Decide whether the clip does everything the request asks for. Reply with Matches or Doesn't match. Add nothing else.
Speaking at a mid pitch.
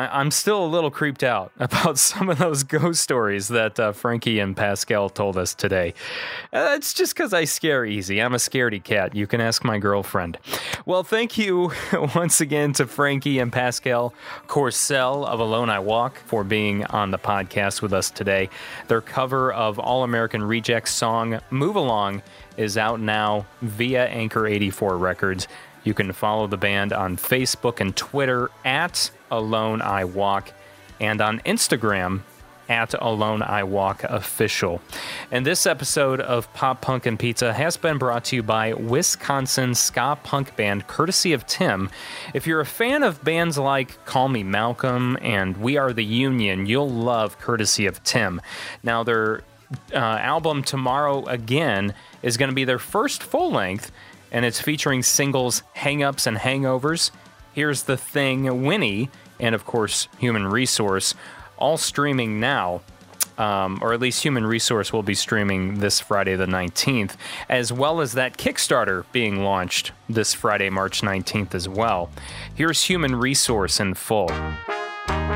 Doesn't match